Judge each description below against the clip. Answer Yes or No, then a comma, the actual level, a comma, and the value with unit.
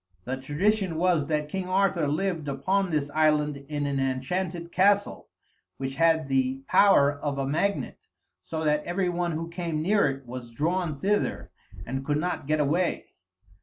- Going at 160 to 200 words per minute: Yes, average, 165 wpm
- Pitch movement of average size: Yes, average, 4.3 semitones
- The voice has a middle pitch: Yes, medium, 155 Hz